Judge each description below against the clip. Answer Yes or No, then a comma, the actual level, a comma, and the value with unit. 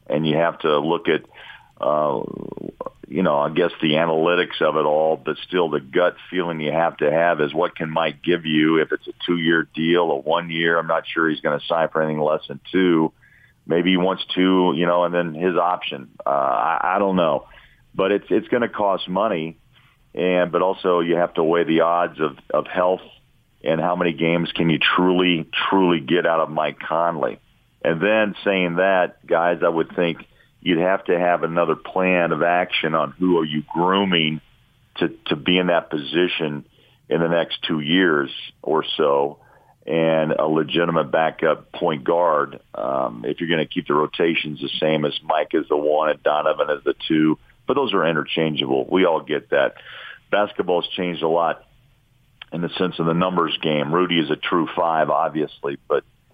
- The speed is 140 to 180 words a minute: No, average, 195 wpm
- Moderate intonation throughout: No, narrow, 2.2 semitones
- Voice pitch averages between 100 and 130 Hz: No, very low, 85 Hz